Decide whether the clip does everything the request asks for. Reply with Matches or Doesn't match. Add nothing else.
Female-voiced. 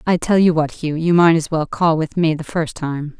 Matches